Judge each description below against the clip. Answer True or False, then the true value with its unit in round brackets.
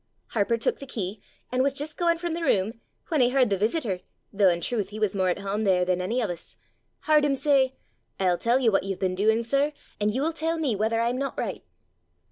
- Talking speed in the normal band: False (235 wpm)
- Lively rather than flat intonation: True (5.9 semitones)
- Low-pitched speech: False (230 Hz)